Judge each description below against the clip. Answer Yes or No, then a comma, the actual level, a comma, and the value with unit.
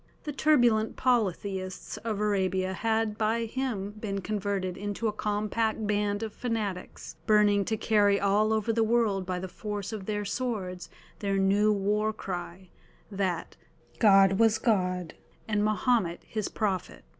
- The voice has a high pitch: Yes, high, 210 Hz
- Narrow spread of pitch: Yes, narrow, 2.3 semitones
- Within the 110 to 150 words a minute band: Yes, average, 145 wpm